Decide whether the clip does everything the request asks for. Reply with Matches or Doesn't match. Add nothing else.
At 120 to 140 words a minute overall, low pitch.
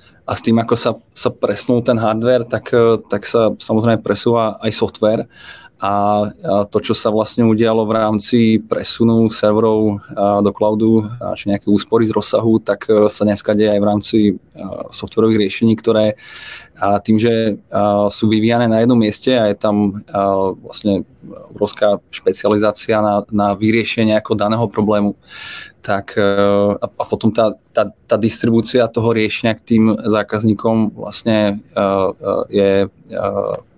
Matches